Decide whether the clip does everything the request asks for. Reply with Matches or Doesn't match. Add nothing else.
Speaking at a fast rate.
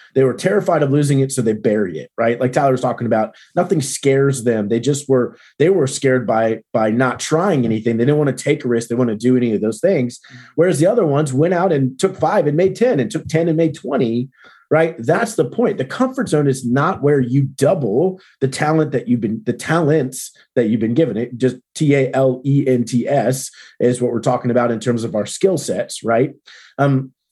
Matches